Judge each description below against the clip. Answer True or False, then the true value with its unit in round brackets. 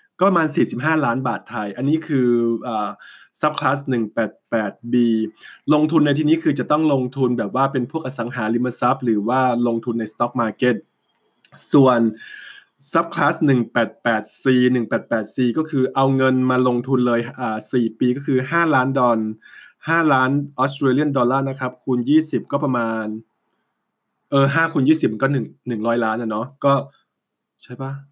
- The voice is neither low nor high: False (130 Hz)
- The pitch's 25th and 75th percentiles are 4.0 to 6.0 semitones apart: False (3.0 semitones)